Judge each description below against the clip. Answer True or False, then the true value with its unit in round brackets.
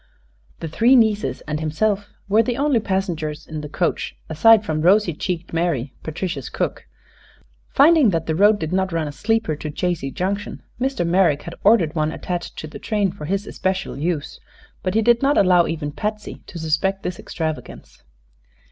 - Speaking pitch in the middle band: True (180 Hz)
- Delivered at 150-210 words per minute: True (175 wpm)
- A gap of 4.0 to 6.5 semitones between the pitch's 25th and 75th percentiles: True (4.9 semitones)